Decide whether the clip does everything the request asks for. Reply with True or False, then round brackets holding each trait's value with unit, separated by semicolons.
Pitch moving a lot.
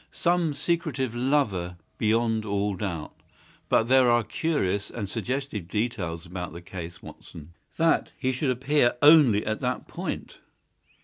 True (6.3 semitones)